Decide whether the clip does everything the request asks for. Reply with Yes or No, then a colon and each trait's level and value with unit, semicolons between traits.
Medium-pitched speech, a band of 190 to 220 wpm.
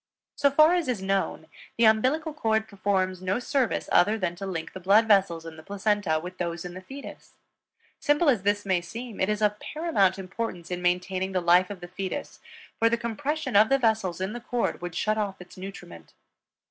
No: high, 200 Hz; average, 200 wpm